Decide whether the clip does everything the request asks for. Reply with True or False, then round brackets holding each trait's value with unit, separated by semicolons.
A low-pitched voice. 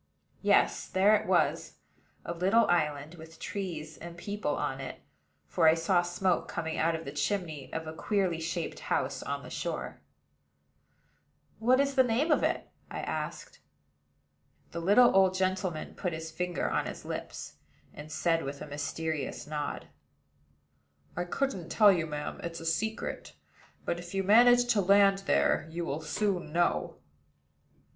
False (175 Hz)